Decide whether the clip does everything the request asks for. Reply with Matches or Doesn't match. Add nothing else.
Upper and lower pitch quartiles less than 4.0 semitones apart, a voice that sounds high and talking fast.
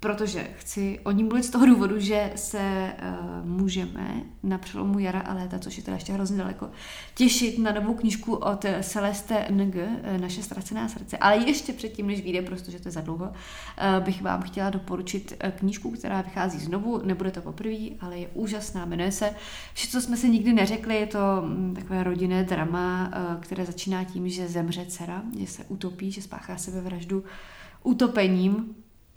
Matches